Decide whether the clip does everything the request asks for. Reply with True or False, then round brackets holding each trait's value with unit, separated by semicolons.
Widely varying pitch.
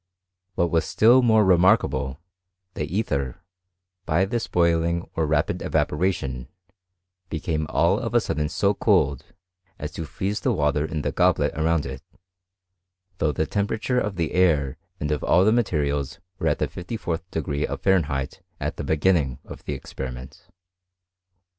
False (4.5 semitones)